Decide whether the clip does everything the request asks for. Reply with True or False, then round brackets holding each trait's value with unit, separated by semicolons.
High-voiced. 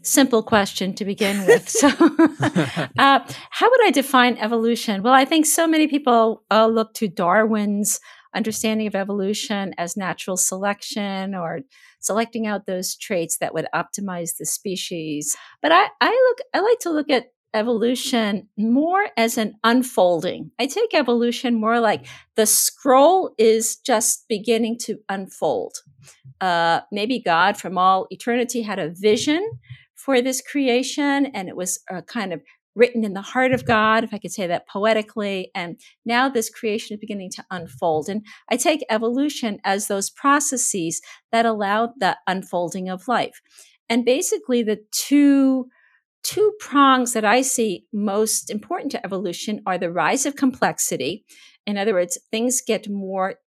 True (220 Hz)